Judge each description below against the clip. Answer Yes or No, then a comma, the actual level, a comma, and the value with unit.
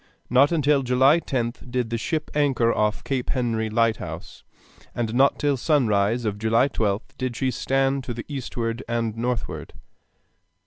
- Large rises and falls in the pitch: No, average, 3.0 semitones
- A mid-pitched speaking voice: No, low, 125 Hz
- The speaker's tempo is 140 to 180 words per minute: Yes, average, 150 wpm